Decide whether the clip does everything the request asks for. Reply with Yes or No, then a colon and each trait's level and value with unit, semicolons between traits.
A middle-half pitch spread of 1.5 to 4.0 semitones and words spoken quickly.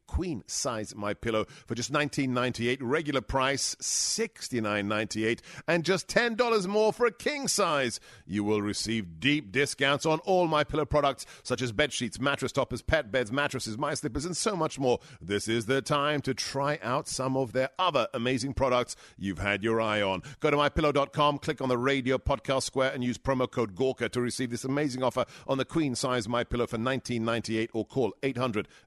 Yes: average, 3.7 semitones; fast, 210 wpm